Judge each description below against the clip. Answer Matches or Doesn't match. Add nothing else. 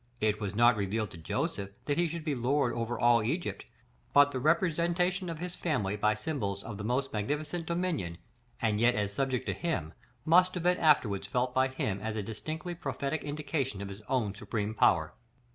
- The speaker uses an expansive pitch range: Matches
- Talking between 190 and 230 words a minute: Matches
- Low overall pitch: Matches